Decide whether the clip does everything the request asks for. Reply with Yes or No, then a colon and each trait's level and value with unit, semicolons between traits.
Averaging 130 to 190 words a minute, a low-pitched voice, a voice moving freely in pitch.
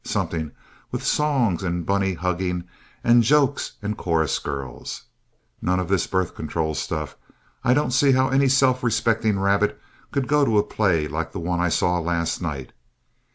Yes: average, 165 wpm; very low, 95 Hz; wide, 6.5 semitones